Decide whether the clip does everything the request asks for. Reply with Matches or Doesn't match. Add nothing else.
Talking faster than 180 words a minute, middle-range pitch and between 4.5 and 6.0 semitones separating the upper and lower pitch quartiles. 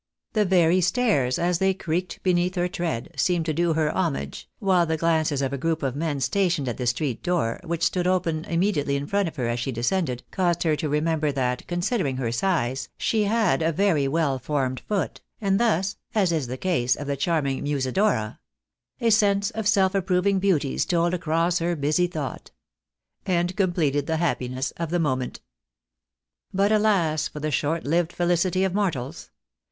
Matches